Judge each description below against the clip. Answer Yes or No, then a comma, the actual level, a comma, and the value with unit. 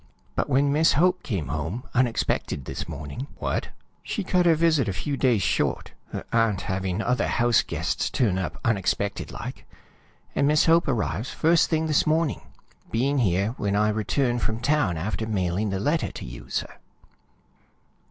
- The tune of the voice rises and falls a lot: Yes, wide, 7.1 semitones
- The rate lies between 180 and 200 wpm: No, average, 170 wpm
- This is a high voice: No, low, 115 Hz